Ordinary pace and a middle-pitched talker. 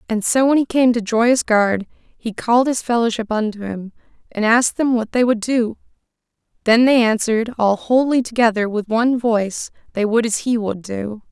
No: average, 190 wpm; high, 230 Hz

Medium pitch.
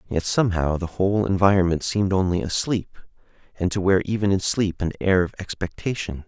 No: very low, 95 Hz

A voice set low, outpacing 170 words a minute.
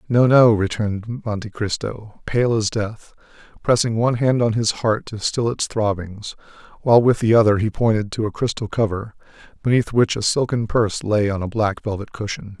Yes: low, 110 Hz; average, 185 wpm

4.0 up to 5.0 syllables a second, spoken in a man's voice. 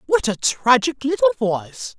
No: 4.7 syllables/s; female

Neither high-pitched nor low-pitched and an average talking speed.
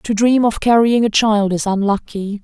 No: high, 215 Hz; average, 195 wpm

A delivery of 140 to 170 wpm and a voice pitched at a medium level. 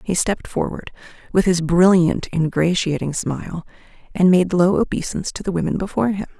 Yes: average, 160 wpm; medium, 175 Hz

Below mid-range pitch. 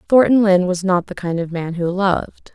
No: medium, 185 Hz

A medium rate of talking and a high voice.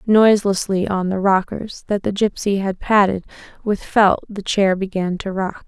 Yes: average, 170 wpm; high, 195 Hz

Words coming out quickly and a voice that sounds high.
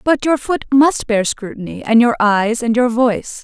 Yes: fast, 210 wpm; high, 240 Hz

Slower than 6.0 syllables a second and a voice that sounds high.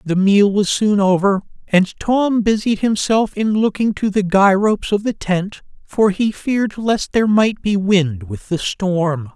Yes: 4.1 syllables/s; high, 200 Hz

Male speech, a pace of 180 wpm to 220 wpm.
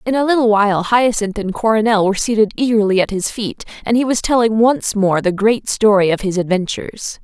No: female; fast, 205 wpm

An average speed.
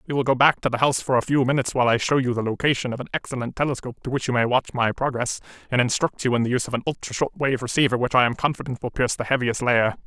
No: fast, 290 wpm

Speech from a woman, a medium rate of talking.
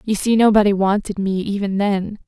Yes: female; average, 185 wpm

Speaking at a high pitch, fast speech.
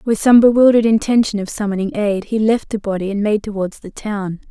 Yes: high, 210 Hz; fast, 215 wpm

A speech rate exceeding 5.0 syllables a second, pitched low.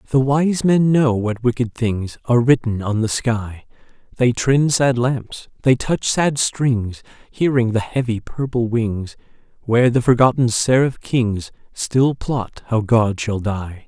No: 3.9 syllables/s; low, 120 Hz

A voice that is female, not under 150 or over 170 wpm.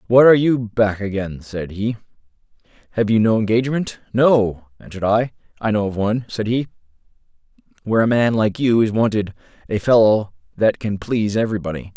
No: male; average, 160 wpm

